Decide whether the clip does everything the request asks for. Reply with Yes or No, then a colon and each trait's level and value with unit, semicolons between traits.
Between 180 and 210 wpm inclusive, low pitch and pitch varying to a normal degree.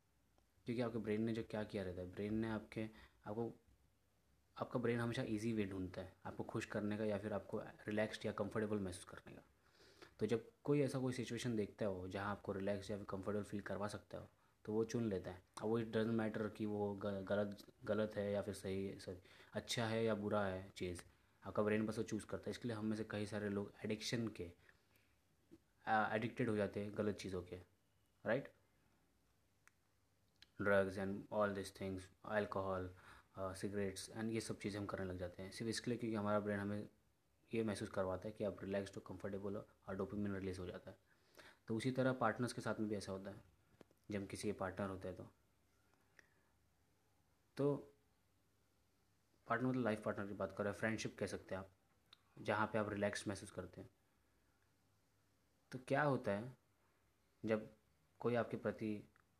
No: fast, 190 wpm; low, 100 Hz; narrow, 2.3 semitones